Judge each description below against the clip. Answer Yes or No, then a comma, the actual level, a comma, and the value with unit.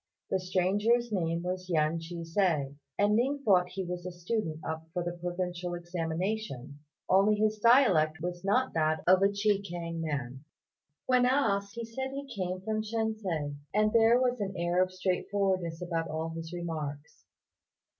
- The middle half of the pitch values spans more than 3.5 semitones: Yes, average, 4.3 semitones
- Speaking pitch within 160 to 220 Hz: Yes, medium, 185 Hz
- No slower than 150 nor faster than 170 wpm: Yes, average, 165 wpm